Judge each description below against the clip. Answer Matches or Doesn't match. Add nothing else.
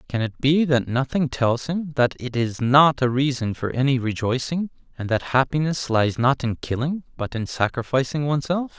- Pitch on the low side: Matches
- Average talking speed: Matches